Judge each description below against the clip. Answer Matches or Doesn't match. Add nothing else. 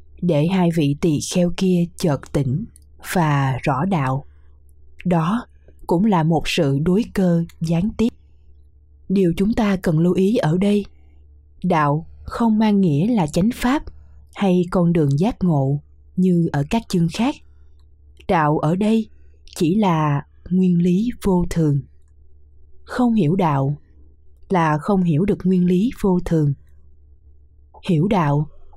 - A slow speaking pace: Matches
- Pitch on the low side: Doesn't match